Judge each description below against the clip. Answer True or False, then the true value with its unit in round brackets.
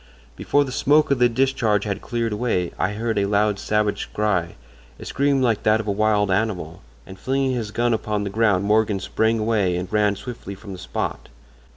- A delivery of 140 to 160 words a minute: False (190 wpm)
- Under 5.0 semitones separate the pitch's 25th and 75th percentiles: True (2.8 semitones)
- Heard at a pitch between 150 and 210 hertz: False (105 Hz)